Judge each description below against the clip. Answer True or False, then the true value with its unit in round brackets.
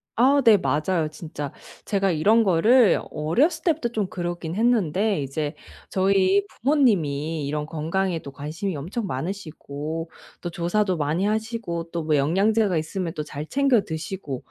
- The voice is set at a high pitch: False (175 Hz)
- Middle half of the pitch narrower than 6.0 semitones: True (5.5 semitones)